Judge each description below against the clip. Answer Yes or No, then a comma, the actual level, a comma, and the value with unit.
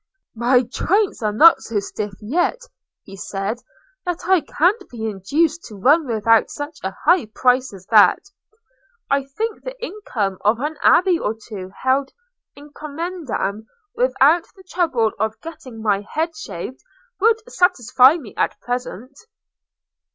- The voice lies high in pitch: Yes, very high, 260 Hz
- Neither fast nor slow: Yes, average, 145 wpm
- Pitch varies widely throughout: Yes, wide, 7.4 semitones